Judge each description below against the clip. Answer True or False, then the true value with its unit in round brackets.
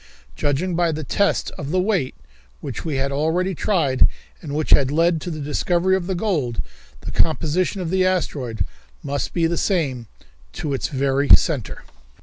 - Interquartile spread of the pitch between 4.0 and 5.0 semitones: True (4.5 semitones)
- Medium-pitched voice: True (155 Hz)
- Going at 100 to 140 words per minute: False (165 wpm)